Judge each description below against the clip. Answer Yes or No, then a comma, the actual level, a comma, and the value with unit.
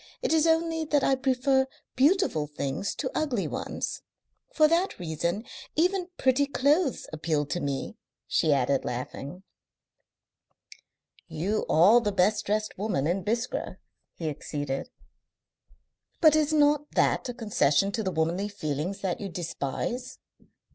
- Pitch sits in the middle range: No, high, 210 Hz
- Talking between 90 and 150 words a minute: Yes, slow, 135 wpm